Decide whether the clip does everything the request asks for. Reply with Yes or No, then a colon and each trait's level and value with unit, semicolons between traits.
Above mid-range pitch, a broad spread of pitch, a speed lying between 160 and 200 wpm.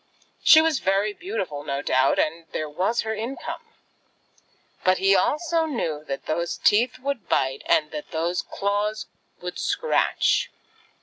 No: high, 195 Hz; wide, 8.2 semitones; average, 140 wpm